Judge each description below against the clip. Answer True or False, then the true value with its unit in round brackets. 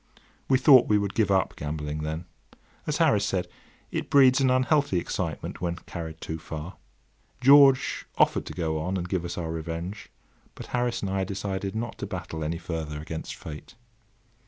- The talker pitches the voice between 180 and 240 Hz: False (90 Hz)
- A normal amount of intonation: False (6.5 semitones)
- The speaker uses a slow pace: False (175 wpm)